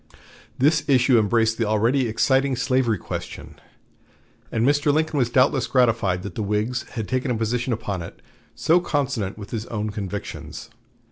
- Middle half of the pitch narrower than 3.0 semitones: No, average, 3.6 semitones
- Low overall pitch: Yes, low, 120 Hz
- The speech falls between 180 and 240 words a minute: No, average, 155 wpm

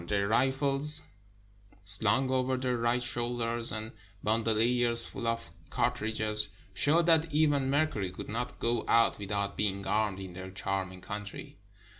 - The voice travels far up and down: No, average, 3.9 semitones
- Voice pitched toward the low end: Yes, low, 115 Hz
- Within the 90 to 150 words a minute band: Yes, average, 140 wpm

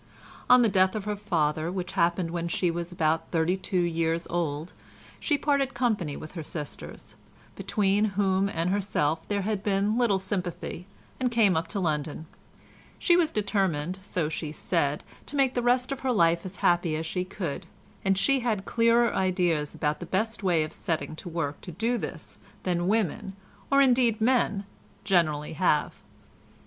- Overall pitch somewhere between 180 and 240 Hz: Yes, medium, 185 Hz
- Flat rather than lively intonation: No, average, 4.4 semitones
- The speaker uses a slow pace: No, average, 175 wpm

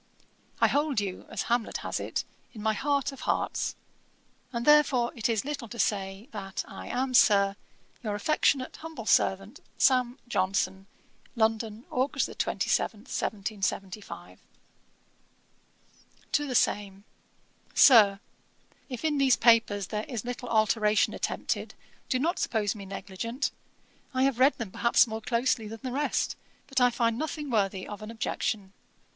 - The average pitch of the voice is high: Yes, high, 230 Hz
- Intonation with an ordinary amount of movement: Yes, average, 3.9 semitones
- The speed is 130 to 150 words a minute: Yes, average, 140 wpm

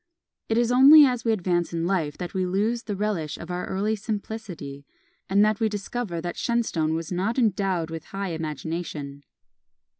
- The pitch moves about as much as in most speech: Yes, average, 4.8 semitones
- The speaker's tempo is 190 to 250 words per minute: No, average, 175 wpm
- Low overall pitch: No, high, 190 Hz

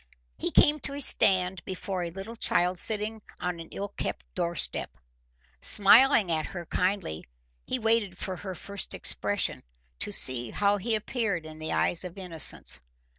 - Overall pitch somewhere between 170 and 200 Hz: Yes, high, 190 Hz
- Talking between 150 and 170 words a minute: Yes, average, 160 wpm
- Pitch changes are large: No, average, 3.5 semitones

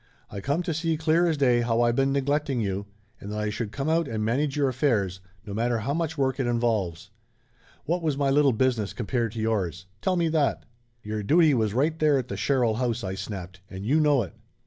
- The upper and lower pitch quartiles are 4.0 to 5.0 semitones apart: No, wide, 5.4 semitones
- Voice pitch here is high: No, low, 125 Hz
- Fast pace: Yes, fast, 230 wpm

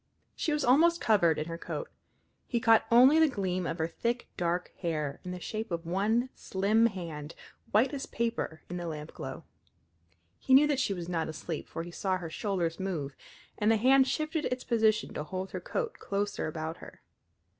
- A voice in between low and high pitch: No, high, 195 Hz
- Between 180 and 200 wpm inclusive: Yes, average, 190 wpm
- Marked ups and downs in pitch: Yes, wide, 6.0 semitones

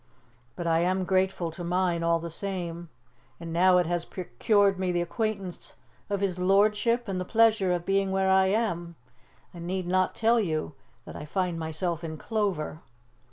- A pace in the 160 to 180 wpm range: Yes, average, 175 wpm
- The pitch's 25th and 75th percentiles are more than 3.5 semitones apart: No, narrow, 2.5 semitones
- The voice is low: No, medium, 185 Hz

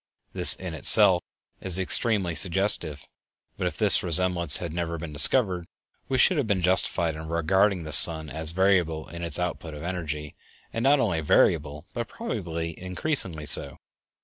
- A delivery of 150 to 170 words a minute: Yes, average, 160 wpm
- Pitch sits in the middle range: No, very low, 85 Hz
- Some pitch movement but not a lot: Yes, average, 3.1 semitones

